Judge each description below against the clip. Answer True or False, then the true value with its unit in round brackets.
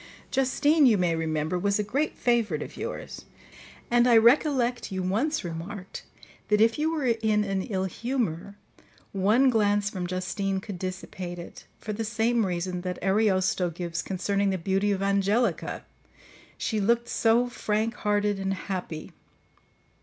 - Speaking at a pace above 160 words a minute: False (145 wpm)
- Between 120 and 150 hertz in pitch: False (205 Hz)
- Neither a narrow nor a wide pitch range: True (3.7 semitones)